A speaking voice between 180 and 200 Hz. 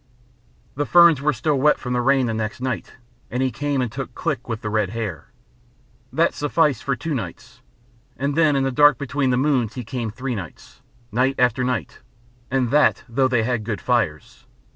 No: low, 130 Hz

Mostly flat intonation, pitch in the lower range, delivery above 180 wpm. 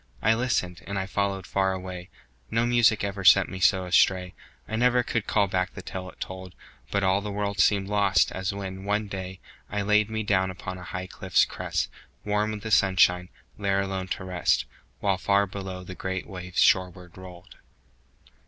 Yes: narrow, 1.7 semitones; very low, 95 Hz; average, 190 wpm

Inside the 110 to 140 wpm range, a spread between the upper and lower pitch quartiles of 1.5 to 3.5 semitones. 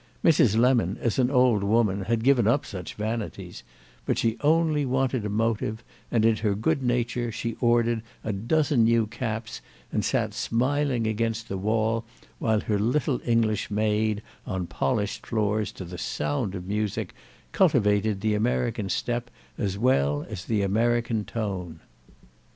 No: average, 150 wpm; narrow, 2.5 semitones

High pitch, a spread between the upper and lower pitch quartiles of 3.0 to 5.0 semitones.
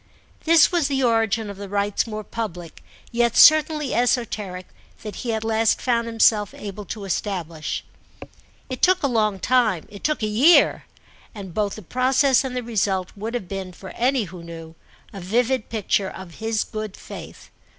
Yes: high, 220 Hz; average, 3.9 semitones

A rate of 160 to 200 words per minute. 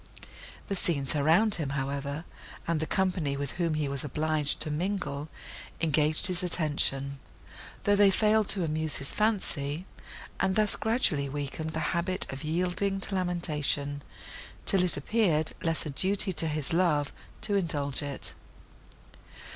No: average, 145 wpm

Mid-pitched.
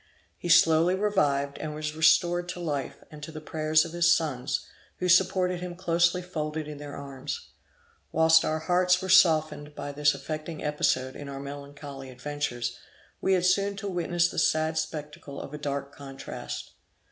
Yes: medium, 155 Hz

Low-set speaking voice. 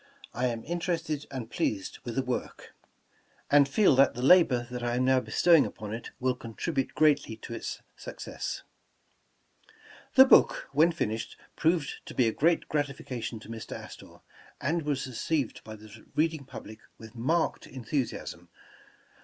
Yes: low, 130 Hz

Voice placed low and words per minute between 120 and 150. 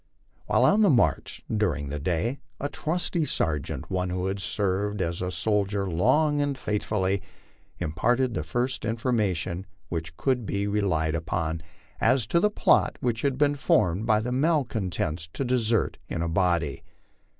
No: low, 105 Hz; average, 160 wpm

